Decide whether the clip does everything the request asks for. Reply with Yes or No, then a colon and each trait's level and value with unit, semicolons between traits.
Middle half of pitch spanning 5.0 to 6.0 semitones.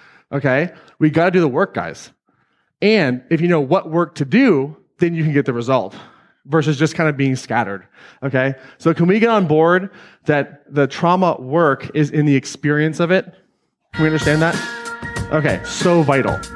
No: average, 3.9 semitones